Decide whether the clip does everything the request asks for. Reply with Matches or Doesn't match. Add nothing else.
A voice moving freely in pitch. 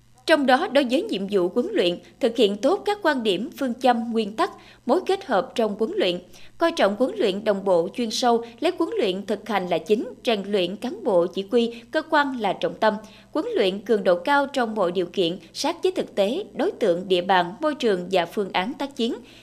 Matches